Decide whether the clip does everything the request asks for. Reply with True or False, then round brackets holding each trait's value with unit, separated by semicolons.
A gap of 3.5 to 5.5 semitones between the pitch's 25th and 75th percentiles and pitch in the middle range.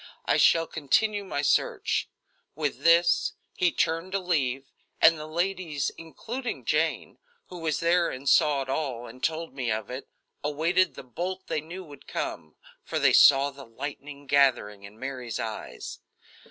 True (4.2 semitones; 150 Hz)